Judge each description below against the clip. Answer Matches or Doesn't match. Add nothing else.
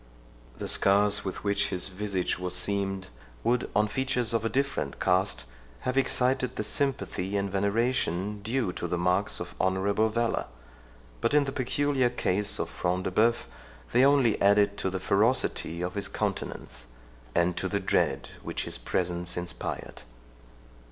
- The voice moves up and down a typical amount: Matches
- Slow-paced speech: Doesn't match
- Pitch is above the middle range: Doesn't match